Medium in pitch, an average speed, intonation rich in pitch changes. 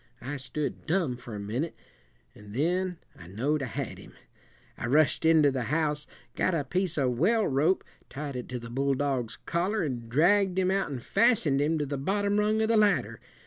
Yes: medium, 150 Hz; average, 195 wpm; wide, 6.1 semitones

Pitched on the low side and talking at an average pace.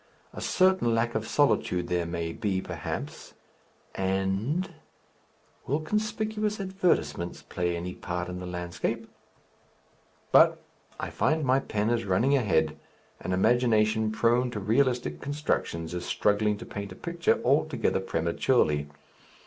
No: low, 110 Hz; slow, 125 wpm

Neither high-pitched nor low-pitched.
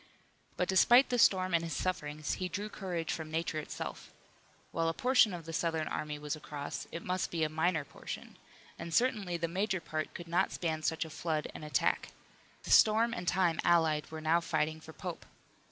Yes: medium, 165 Hz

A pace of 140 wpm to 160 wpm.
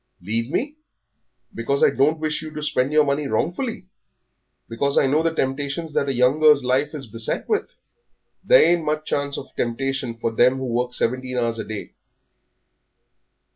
No: average, 175 wpm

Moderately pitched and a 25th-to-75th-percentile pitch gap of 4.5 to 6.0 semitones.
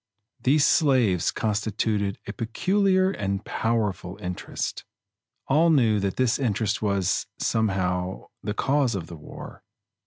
No: low, 110 Hz; average, 5.1 semitones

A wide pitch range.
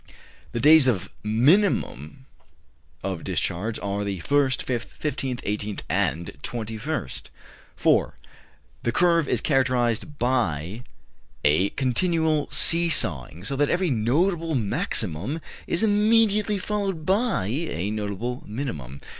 Yes: wide, 8.0 semitones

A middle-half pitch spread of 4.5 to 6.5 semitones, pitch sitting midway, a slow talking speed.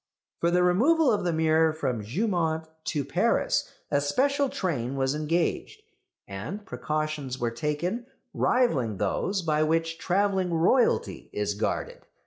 Yes: average, 5.1 semitones; medium, 165 Hz; slow, 130 wpm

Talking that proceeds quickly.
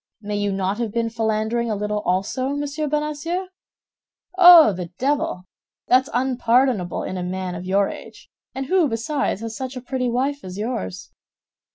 No: average, 165 wpm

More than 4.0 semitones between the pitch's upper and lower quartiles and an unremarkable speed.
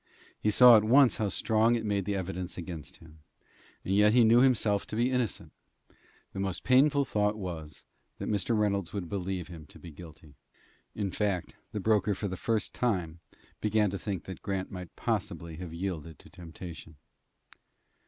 No: average, 3.6 semitones; average, 175 wpm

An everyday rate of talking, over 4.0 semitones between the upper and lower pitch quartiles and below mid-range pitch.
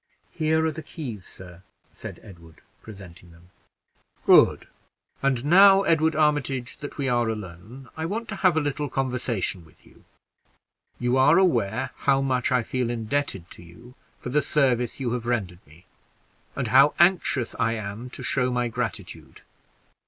Yes: average, 160 wpm; average, 5.1 semitones; low, 125 Hz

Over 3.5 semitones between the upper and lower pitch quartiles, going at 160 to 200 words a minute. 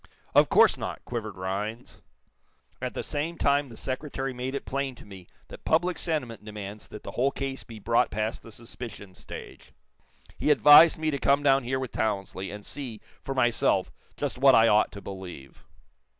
Yes: average, 4.7 semitones; average, 180 wpm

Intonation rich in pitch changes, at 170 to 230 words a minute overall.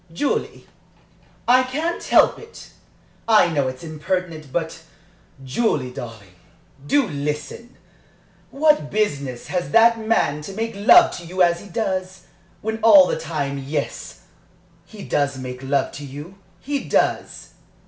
No: wide, 7.7 semitones; slow, 135 wpm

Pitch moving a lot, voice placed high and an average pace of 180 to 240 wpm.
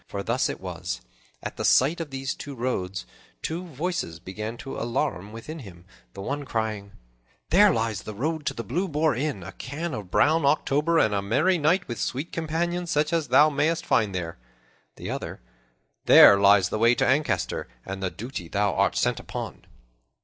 No: wide, 7.5 semitones; low, 130 Hz; average, 185 wpm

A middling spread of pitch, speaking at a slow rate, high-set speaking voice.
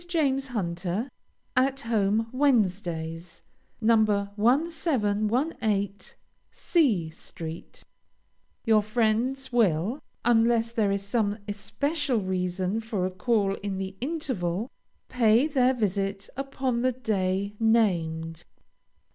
Yes: average, 4.7 semitones; slow, 95 wpm; high, 215 Hz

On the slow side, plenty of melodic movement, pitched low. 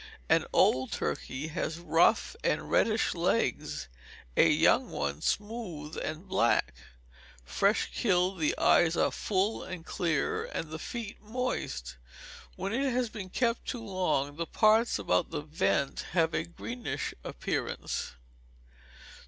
No: slow, 130 wpm; wide, 6.0 semitones; medium, 180 Hz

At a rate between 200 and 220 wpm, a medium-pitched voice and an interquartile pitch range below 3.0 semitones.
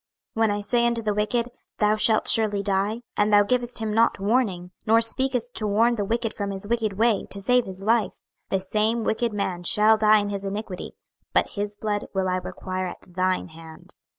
No: fast, 205 wpm; high, 210 Hz; narrow, 2.6 semitones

